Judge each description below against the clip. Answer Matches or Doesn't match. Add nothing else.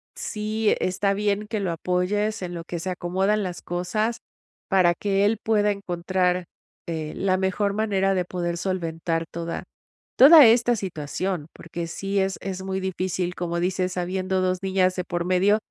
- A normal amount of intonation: Doesn't match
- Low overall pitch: Doesn't match